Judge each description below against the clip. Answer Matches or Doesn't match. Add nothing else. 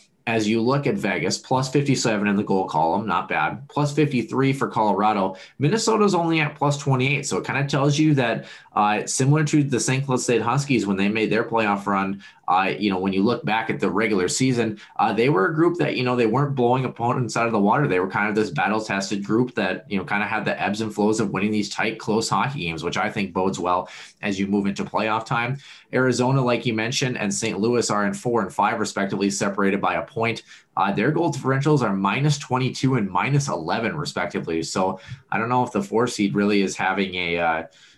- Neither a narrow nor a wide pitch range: Matches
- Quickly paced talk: Matches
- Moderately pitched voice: Doesn't match